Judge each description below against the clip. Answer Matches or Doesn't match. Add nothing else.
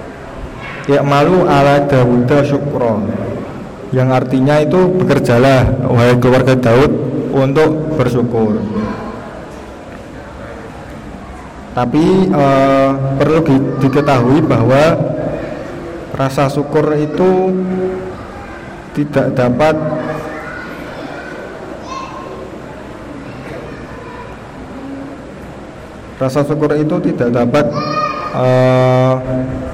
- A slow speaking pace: Matches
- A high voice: Doesn't match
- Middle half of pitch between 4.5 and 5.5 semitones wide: Doesn't match